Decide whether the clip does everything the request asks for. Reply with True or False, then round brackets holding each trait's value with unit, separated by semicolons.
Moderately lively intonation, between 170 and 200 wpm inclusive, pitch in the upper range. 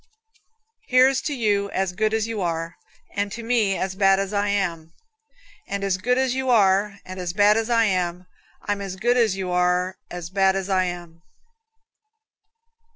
True (3.0 semitones; 180 wpm; 195 Hz)